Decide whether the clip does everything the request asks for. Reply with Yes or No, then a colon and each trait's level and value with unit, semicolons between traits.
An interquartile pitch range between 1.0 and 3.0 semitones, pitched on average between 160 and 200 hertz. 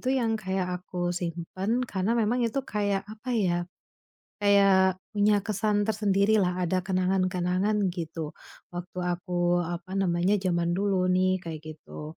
Yes: narrow, 2.6 semitones; medium, 185 Hz